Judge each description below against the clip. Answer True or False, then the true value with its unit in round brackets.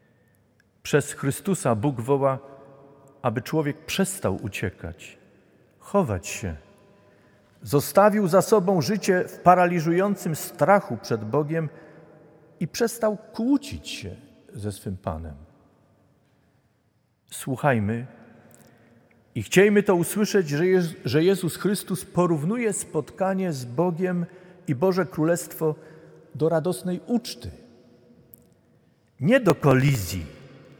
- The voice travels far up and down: True (6.0 semitones)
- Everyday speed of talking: False (90 wpm)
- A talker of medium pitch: True (160 Hz)